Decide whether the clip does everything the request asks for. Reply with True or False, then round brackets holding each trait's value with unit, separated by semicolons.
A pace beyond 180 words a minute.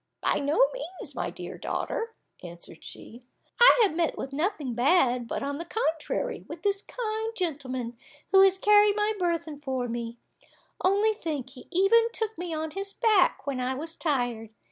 False (170 wpm)